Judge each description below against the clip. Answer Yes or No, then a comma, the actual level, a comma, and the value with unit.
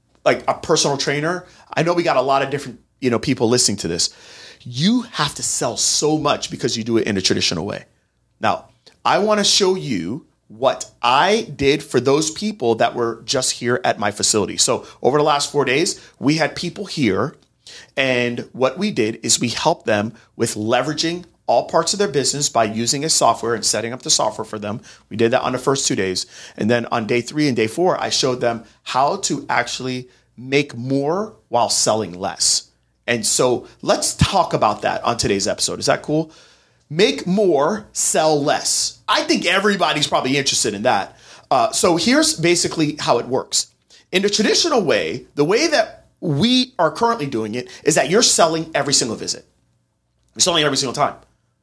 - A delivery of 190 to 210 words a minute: Yes, average, 195 wpm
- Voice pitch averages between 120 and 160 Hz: Yes, medium, 140 Hz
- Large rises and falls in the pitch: Yes, wide, 6.4 semitones